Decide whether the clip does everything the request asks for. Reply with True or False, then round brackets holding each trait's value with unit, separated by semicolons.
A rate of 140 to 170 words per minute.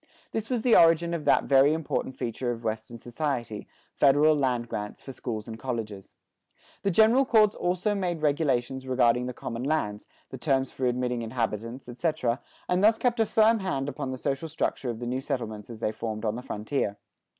False (190 wpm)